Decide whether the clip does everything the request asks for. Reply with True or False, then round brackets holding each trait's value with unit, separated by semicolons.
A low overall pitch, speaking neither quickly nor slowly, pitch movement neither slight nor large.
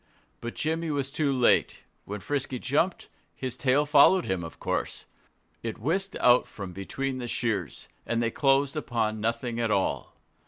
True (125 Hz; 160 wpm; 4.1 semitones)